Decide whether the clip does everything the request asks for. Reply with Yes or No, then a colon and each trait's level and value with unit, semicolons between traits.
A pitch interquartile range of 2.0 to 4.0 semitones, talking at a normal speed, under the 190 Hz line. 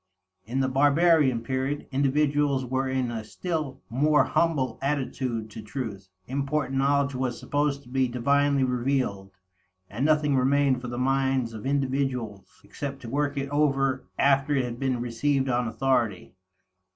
Yes: narrow, 2.4 semitones; average, 150 wpm; low, 135 Hz